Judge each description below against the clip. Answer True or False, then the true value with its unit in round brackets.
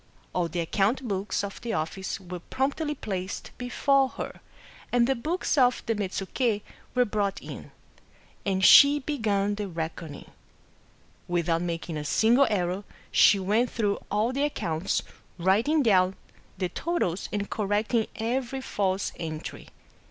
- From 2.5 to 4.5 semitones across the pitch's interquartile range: False (5.1 semitones)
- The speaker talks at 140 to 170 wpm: True (145 wpm)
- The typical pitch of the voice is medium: False (205 Hz)